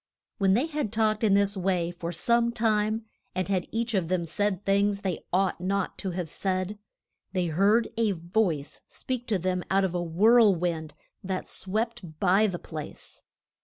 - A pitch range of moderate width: Yes, average, 3.3 semitones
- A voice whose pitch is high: Yes, high, 195 Hz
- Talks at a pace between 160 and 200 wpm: Yes, average, 175 wpm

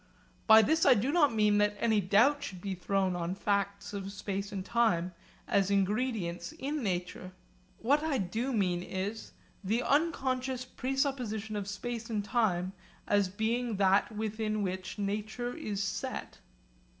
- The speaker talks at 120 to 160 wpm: Yes, average, 150 wpm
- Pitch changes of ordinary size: Yes, average, 3.7 semitones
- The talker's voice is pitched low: No, high, 210 Hz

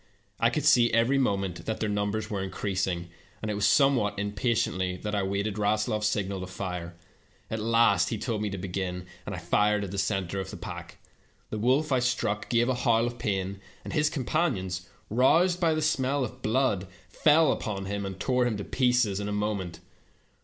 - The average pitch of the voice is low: Yes, low, 105 Hz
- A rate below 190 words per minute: No, average, 195 wpm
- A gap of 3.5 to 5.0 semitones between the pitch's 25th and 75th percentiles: Yes, average, 4.0 semitones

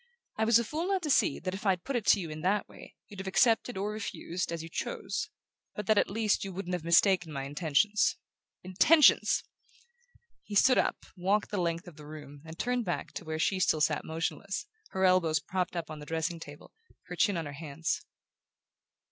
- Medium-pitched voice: Yes, medium, 180 Hz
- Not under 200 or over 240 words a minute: Yes, fast, 205 wpm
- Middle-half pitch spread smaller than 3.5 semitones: No, average, 4.4 semitones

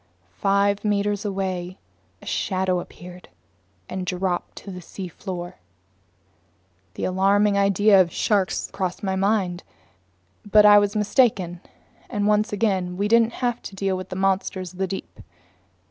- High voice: Yes, high, 195 Hz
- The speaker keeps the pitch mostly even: Yes, narrow, 1.9 semitones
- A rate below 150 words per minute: Yes, slow, 135 wpm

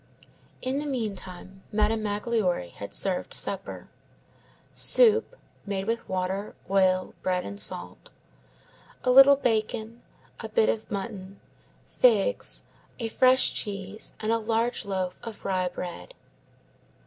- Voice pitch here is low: No, high, 210 Hz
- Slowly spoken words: Yes, slow, 120 wpm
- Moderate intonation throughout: Yes, average, 3.9 semitones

